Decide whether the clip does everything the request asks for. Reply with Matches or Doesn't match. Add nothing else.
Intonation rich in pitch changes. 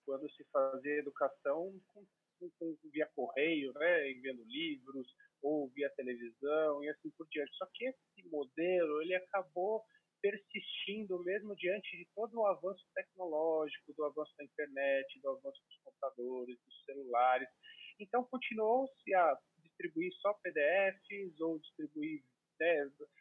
Matches